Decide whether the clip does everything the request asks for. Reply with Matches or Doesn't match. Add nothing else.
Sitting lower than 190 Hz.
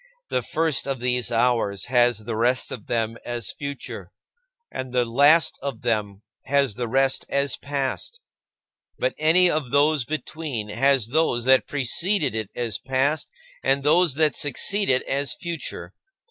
Matches